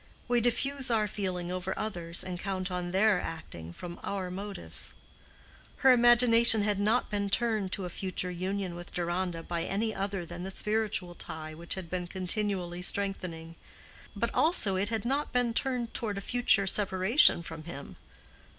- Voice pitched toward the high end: Yes, high, 195 Hz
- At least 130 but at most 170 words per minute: Yes, average, 165 wpm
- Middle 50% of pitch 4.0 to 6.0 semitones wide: No, average, 3.6 semitones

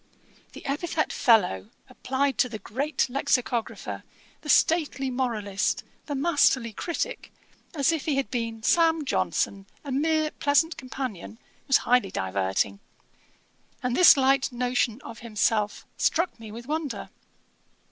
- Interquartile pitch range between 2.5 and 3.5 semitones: No, average, 4.6 semitones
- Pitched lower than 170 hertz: No, very high, 260 Hz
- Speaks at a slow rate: Yes, slow, 125 wpm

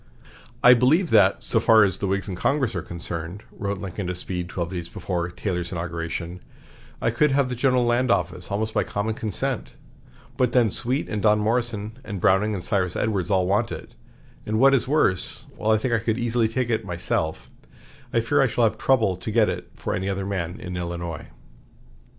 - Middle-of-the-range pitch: No, low, 105 Hz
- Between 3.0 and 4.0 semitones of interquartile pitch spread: No, average, 4.6 semitones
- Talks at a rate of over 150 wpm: Yes, average, 200 wpm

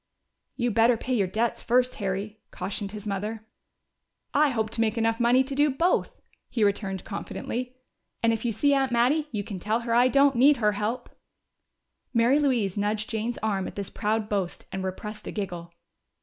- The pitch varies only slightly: No, average, 3.2 semitones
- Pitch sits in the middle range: No, high, 225 Hz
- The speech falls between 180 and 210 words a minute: Yes, average, 185 wpm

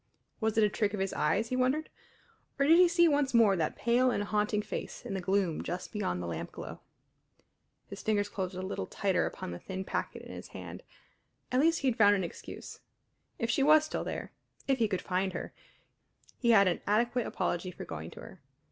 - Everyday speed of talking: No, fast, 210 wpm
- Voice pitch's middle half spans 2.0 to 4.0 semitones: No, average, 5.1 semitones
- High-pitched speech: Yes, high, 210 Hz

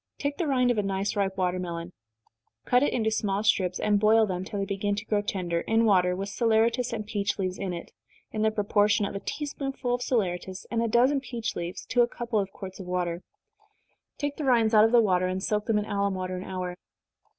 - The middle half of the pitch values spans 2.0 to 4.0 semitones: Yes, average, 3.5 semitones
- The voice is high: Yes, high, 205 Hz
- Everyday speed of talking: No, fast, 235 wpm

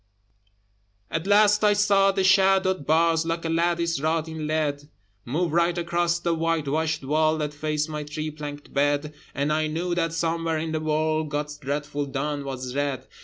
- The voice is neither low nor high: Yes, medium, 155 Hz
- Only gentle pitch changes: Yes, narrow, 2.3 semitones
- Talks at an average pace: Yes, average, 170 wpm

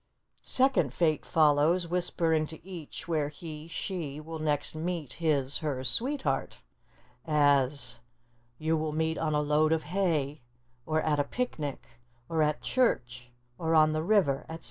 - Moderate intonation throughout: No, narrow, 2.2 semitones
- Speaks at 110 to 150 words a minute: Yes, average, 145 wpm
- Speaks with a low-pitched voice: No, medium, 155 Hz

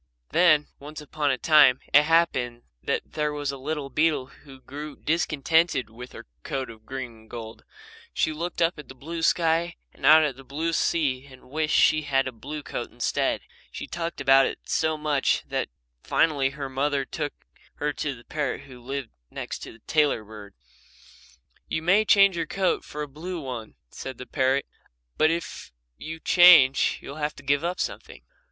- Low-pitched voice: No, medium, 145 Hz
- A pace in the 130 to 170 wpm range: No, average, 185 wpm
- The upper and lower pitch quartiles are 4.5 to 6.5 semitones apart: No, average, 3.2 semitones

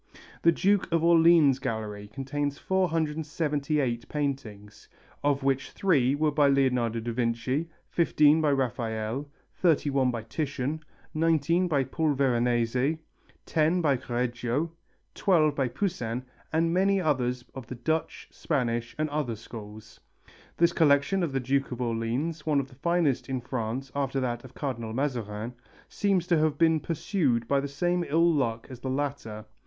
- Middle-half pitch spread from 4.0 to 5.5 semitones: Yes, average, 4.6 semitones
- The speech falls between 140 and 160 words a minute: Yes, average, 150 wpm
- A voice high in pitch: No, medium, 140 Hz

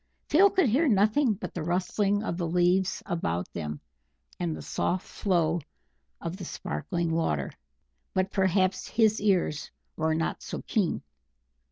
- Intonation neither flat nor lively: Yes, average, 3.8 semitones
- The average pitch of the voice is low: No, medium, 185 Hz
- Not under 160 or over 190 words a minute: No, average, 145 wpm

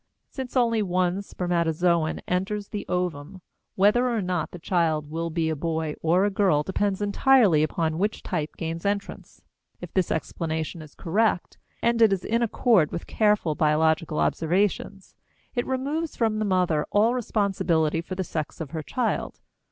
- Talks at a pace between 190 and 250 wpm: No, average, 160 wpm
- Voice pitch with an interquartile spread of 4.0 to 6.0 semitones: Yes, average, 4.5 semitones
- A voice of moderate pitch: Yes, medium, 180 Hz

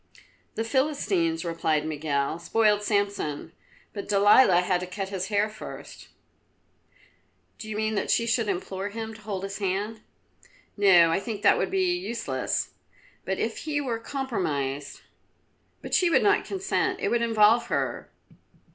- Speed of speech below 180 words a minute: Yes, average, 155 wpm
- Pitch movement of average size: Yes, average, 4.1 semitones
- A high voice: Yes, high, 205 Hz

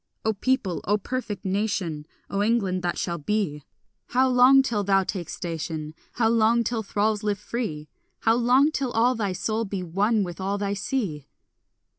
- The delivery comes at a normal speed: Yes, average, 170 wpm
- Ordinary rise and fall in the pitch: Yes, average, 4.1 semitones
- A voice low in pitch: No, high, 205 Hz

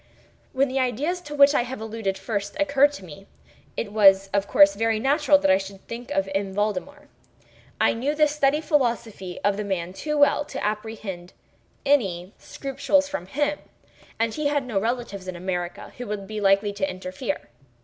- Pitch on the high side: Yes, high, 220 Hz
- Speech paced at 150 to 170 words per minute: No, average, 180 wpm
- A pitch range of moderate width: No, wide, 6.5 semitones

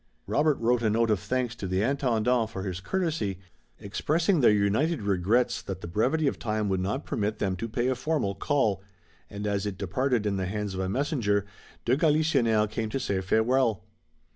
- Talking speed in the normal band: Yes, average, 190 wpm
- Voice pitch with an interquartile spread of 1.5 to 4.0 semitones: No, average, 4.6 semitones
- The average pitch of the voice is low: Yes, low, 110 Hz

